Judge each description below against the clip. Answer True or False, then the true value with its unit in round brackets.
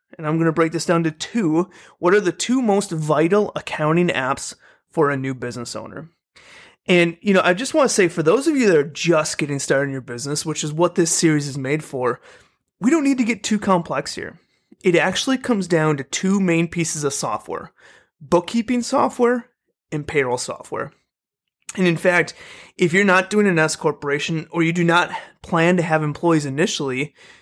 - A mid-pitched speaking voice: True (170 Hz)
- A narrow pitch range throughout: False (4.0 semitones)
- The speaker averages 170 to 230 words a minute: True (200 wpm)